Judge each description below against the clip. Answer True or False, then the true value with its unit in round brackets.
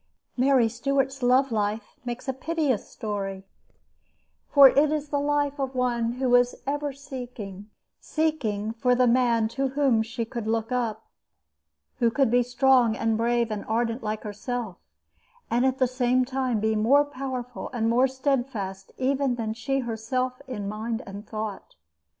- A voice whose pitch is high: True (245 Hz)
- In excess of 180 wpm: False (155 wpm)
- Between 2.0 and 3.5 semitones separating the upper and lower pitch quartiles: True (3.1 semitones)